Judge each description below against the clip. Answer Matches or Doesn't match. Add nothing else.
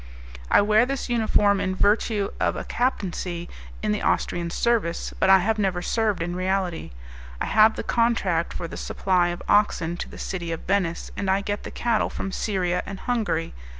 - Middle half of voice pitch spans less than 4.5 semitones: Matches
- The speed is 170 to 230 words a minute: Matches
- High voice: Matches